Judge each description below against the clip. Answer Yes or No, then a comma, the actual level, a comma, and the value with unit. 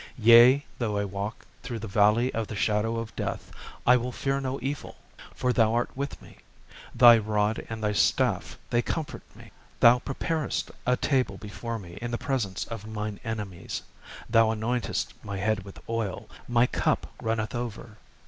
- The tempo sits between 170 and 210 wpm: Yes, average, 175 wpm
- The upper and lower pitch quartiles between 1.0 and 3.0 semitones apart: Yes, narrow, 2.5 semitones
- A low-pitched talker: Yes, low, 115 Hz